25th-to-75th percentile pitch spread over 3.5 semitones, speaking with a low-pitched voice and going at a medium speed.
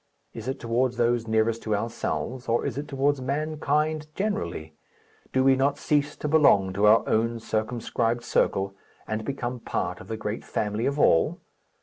Yes: average, 4.2 semitones; low, 120 Hz; average, 165 wpm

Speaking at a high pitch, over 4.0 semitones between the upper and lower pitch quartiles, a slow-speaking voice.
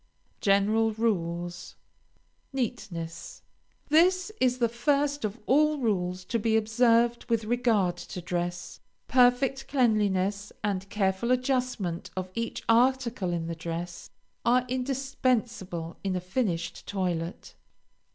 Yes: high, 220 Hz; wide, 5.5 semitones; slow, 110 wpm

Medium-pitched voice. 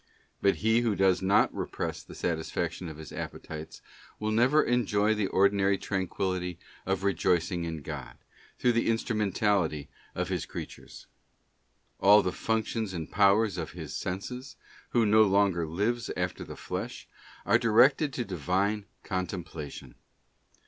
No: low, 100 Hz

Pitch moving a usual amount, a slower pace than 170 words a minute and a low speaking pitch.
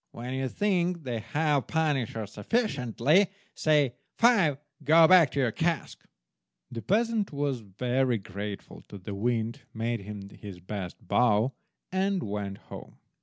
No: wide, 7.2 semitones; average, 140 wpm; low, 125 Hz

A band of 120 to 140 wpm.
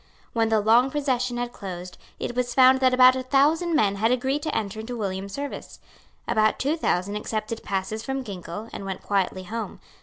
No: average, 190 wpm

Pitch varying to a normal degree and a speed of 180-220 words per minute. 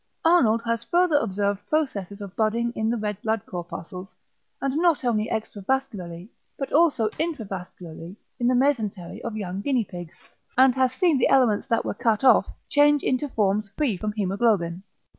No: average, 5.0 semitones; average, 160 wpm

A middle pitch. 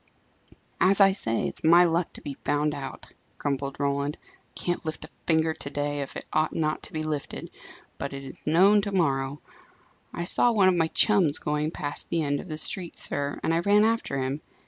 Yes: medium, 155 Hz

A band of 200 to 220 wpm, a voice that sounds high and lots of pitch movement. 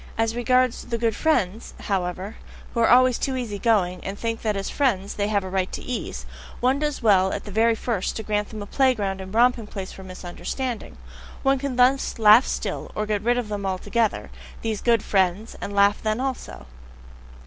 No: fast, 205 wpm; high, 220 Hz; average, 3.7 semitones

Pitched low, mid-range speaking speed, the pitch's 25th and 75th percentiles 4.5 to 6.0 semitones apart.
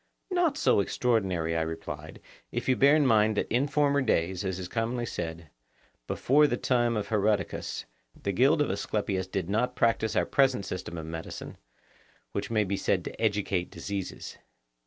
Yes: low, 105 Hz; average, 170 wpm; average, 5.0 semitones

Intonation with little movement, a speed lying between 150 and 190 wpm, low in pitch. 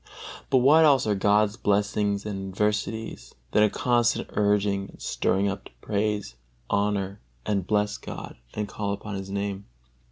Yes: narrow, 1.2 semitones; average, 160 wpm; low, 105 Hz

